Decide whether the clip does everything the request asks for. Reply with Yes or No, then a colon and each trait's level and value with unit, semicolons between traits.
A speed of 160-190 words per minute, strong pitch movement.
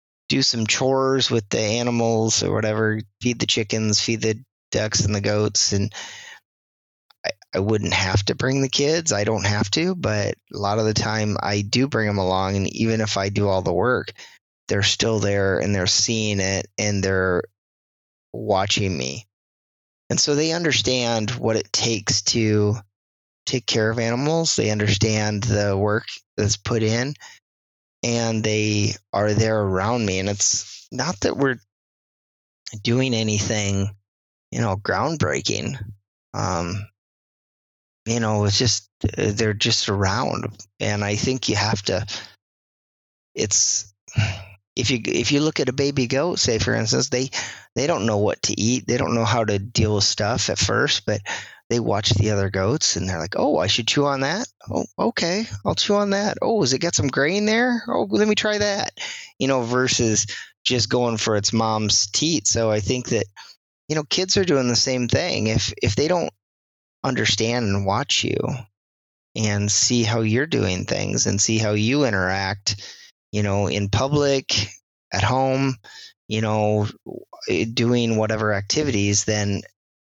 No: average, 170 wpm; average, 3.6 semitones